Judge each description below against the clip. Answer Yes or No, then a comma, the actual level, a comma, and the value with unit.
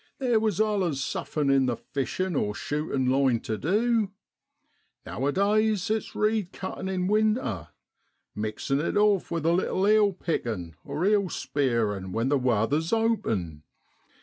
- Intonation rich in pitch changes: Yes, wide, 8.6 semitones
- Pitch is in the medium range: Yes, medium, 165 Hz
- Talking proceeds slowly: No, average, 145 wpm